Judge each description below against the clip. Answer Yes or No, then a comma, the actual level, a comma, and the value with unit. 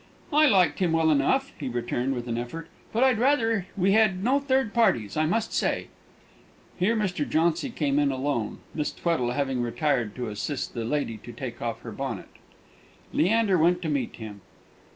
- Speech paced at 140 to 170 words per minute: No, average, 180 wpm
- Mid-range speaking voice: Yes, medium, 160 Hz